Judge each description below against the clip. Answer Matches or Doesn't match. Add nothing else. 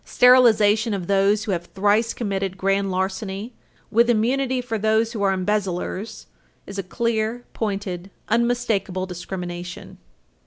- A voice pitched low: Doesn't match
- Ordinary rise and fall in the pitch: Matches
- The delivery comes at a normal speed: Doesn't match